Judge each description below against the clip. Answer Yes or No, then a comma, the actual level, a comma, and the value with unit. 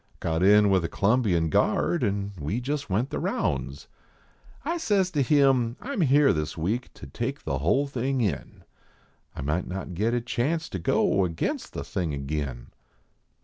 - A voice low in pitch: Yes, low, 105 Hz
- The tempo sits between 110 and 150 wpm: No, average, 180 wpm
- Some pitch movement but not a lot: No, wide, 8.4 semitones